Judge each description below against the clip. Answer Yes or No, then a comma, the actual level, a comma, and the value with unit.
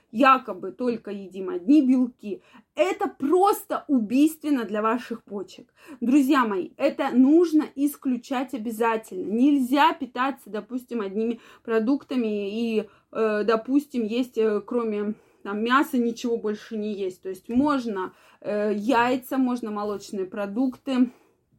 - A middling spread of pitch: Yes, average, 4.4 semitones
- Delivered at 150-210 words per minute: No, slow, 110 wpm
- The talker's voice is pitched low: No, high, 240 Hz